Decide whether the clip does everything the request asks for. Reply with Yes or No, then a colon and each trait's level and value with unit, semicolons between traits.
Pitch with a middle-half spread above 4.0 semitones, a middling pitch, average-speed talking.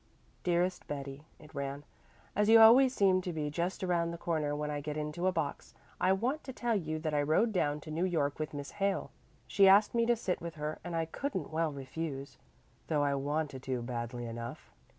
No: average, 4.4 semitones; medium, 160 Hz; fast, 210 wpm